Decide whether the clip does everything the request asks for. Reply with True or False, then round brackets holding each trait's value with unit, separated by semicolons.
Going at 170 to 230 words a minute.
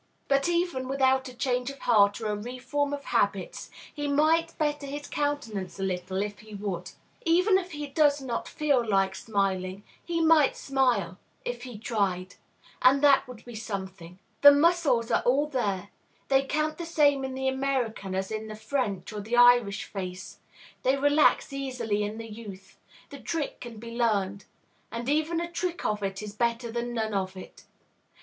True (175 wpm)